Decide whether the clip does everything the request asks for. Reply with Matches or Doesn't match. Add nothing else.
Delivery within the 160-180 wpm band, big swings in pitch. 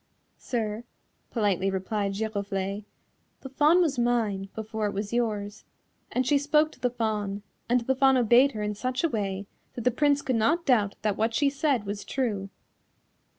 Doesn't match